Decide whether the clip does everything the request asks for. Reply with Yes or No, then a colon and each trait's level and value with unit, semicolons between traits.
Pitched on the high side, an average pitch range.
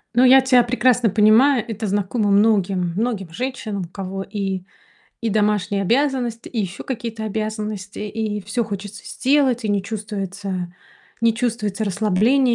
Yes: high, 215 Hz; average, 3.1 semitones